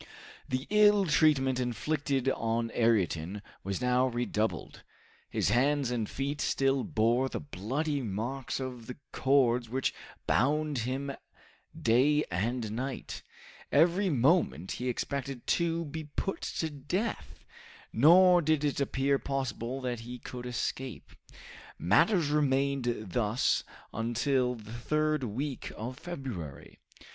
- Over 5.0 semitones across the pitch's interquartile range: No, average, 3.8 semitones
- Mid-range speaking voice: No, low, 130 Hz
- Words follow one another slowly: Yes, slow, 120 wpm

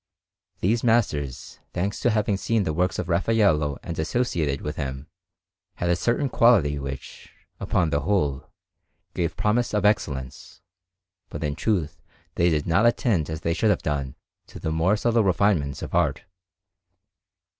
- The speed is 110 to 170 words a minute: Yes, average, 155 wpm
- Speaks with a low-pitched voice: Yes, very low, 85 Hz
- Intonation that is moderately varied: No, wide, 6.1 semitones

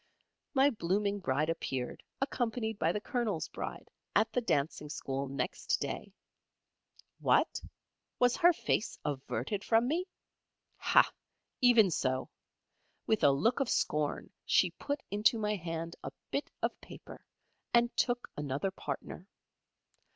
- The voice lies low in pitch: No, high, 205 Hz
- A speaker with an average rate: No, slow, 130 wpm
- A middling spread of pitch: No, wide, 8.1 semitones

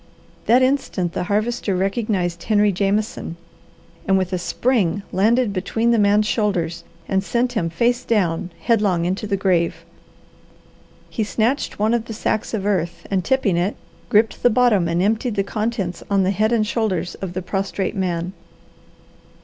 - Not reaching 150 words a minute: No, average, 160 wpm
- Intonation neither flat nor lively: Yes, average, 3.5 semitones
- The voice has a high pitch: Yes, high, 200 Hz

